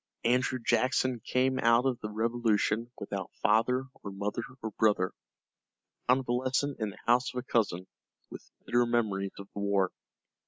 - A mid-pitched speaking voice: No, low, 115 Hz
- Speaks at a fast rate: No, average, 155 wpm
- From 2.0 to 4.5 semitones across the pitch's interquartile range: Yes, average, 3.5 semitones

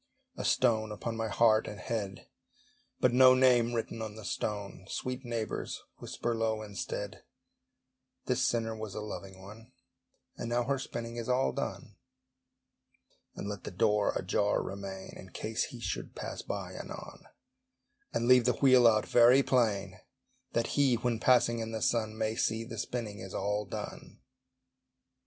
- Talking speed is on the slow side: No, average, 155 wpm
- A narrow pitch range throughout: Yes, narrow, 2.3 semitones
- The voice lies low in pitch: Yes, low, 115 Hz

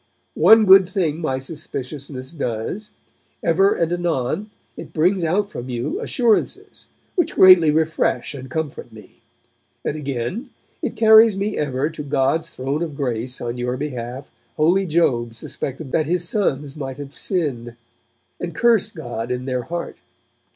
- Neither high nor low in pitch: Yes, medium, 150 Hz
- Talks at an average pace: Yes, average, 145 wpm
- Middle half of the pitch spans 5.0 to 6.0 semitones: Yes, wide, 5.6 semitones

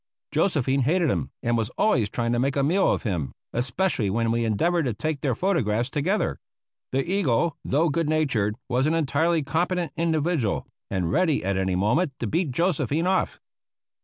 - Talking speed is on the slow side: No, average, 175 wpm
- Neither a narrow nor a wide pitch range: No, wide, 6.3 semitones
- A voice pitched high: No, medium, 140 Hz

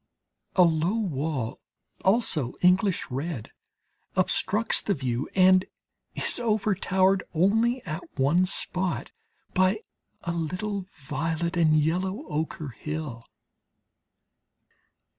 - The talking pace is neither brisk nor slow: No, slow, 95 wpm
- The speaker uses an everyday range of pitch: Yes, average, 4.0 semitones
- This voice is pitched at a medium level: Yes, medium, 175 Hz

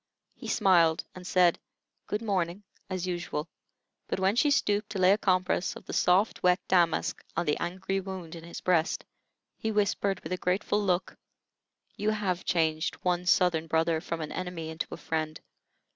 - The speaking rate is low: No, average, 175 wpm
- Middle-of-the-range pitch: Yes, medium, 180 Hz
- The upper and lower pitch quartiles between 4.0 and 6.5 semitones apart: No, narrow, 2.5 semitones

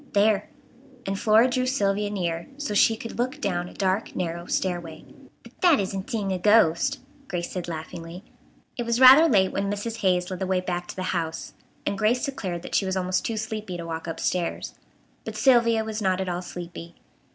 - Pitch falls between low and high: No, high, 195 Hz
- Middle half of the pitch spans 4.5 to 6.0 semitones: No, average, 4.0 semitones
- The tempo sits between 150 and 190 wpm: No, average, 200 wpm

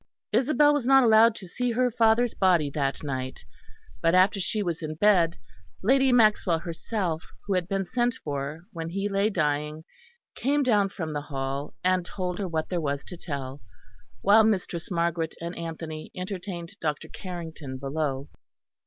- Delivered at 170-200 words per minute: No, average, 160 wpm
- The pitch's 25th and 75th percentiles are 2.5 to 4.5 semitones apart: No, average, 5.2 semitones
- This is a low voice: No, medium, 175 Hz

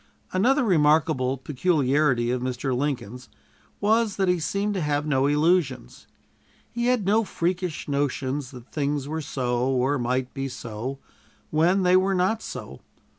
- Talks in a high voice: No, medium, 145 Hz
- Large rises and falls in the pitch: Yes, wide, 6.0 semitones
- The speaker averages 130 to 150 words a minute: Yes, average, 145 wpm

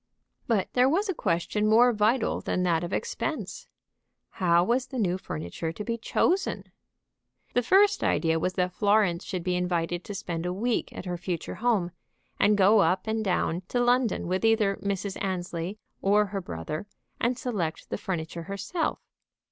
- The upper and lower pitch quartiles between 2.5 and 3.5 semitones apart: No, average, 4.4 semitones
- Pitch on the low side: No, high, 195 Hz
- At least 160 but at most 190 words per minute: Yes, average, 170 wpm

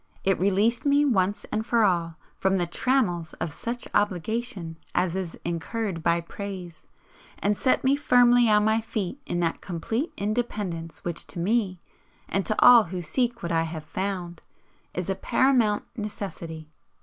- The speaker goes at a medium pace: Yes, average, 160 wpm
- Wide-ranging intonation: No, average, 4.9 semitones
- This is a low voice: No, high, 195 Hz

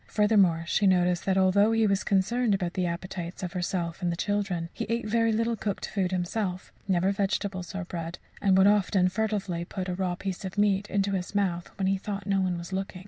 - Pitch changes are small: Yes, narrow, 2.2 semitones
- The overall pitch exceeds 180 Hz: Yes, high, 190 Hz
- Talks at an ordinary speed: No, fast, 215 wpm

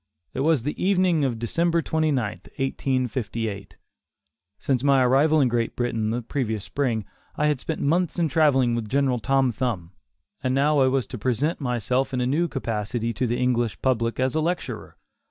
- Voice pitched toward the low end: Yes, low, 130 Hz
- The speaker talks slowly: No, average, 175 wpm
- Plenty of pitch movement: No, average, 3.8 semitones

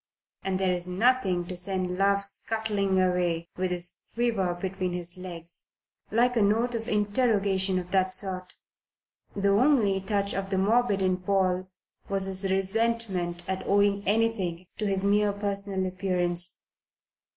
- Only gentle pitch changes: Yes, narrow, 2.0 semitones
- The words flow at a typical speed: Yes, average, 145 wpm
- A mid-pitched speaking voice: No, high, 195 Hz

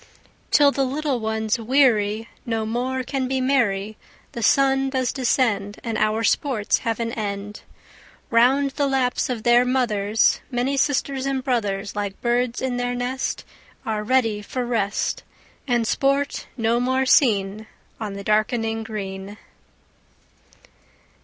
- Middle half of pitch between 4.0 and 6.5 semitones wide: No, average, 3.5 semitones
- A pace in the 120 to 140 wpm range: Yes, slow, 135 wpm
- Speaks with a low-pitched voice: No, high, 240 Hz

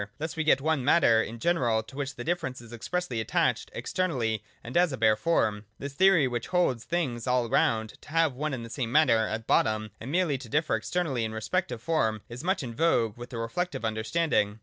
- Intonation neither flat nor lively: No, wide, 6.1 semitones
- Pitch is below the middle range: Yes, low, 125 Hz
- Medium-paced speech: No, fast, 215 wpm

